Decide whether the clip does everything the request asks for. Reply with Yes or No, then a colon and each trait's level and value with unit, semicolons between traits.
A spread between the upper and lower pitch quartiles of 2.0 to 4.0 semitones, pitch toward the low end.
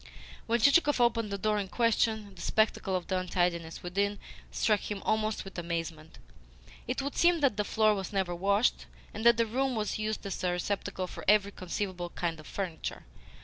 No: average, 3.3 semitones; high, 200 Hz